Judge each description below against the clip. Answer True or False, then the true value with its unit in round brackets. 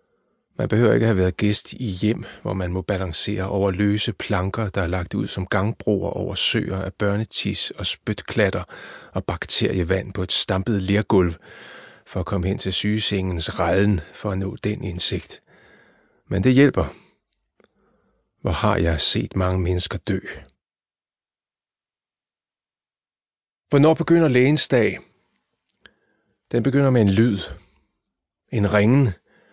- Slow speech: True (135 wpm)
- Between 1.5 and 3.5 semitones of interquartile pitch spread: True (2.7 semitones)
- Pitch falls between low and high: False (100 Hz)